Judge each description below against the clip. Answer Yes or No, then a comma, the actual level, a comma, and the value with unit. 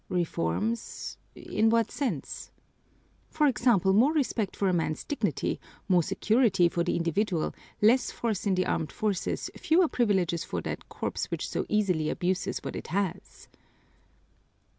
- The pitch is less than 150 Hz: No, high, 200 Hz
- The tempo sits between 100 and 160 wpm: Yes, average, 140 wpm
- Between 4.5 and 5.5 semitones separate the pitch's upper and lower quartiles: Yes, average, 4.8 semitones